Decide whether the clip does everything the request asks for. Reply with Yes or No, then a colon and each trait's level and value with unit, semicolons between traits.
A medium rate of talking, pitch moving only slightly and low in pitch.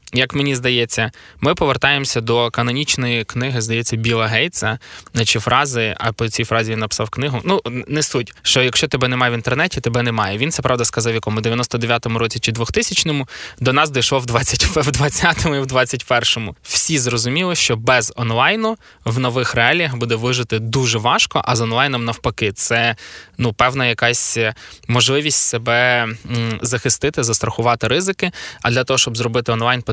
No: fast, 160 wpm; narrow, 2.3 semitones; low, 120 Hz